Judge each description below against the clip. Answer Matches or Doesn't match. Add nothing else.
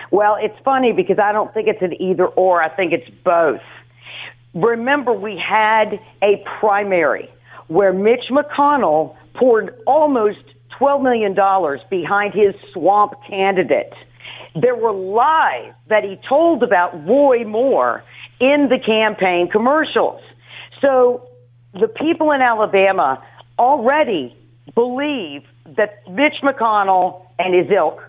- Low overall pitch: Doesn't match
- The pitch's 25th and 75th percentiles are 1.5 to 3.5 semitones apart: Doesn't match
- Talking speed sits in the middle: Doesn't match